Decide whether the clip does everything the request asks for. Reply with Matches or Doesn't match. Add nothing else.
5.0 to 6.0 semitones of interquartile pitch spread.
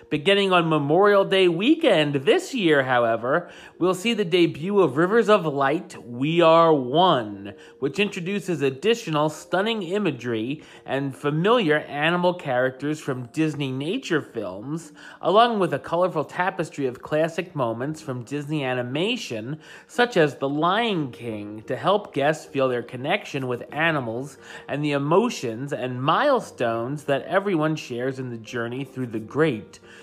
Matches